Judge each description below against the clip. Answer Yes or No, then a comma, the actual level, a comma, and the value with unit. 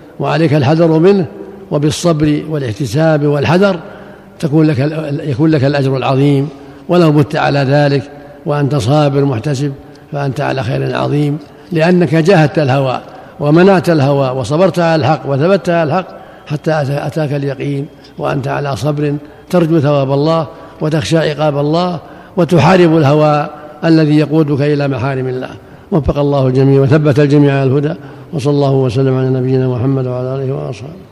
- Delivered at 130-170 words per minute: Yes, fast, 135 wpm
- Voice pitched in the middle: Yes, medium, 150 Hz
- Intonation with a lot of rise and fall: No, narrow, 2.4 semitones